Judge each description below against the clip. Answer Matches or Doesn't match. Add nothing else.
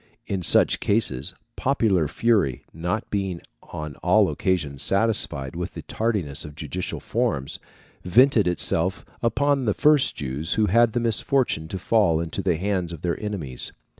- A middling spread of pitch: Doesn't match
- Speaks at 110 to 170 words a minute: Matches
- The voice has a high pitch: Doesn't match